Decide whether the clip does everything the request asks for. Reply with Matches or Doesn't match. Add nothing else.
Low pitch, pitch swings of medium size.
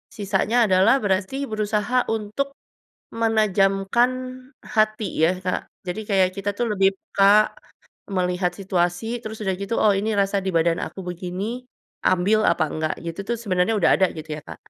Doesn't match